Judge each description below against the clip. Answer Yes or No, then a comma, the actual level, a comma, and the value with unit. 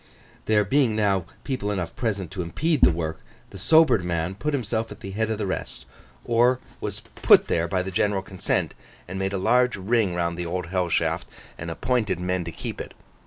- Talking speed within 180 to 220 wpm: Yes, fast, 205 wpm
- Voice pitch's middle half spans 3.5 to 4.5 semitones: Yes, average, 4.0 semitones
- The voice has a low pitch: Yes, very low, 95 Hz